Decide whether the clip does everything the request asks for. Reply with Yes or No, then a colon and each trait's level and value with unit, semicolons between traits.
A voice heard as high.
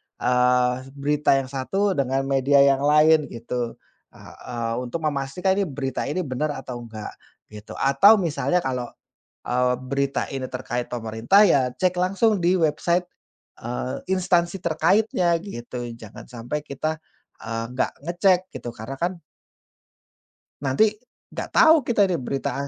No: medium, 140 Hz